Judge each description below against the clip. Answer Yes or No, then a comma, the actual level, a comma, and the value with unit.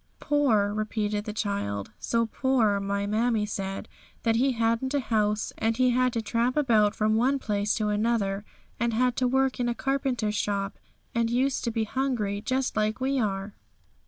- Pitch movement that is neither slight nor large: Yes, average, 3.3 semitones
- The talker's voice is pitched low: No, high, 225 Hz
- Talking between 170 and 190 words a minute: Yes, average, 175 wpm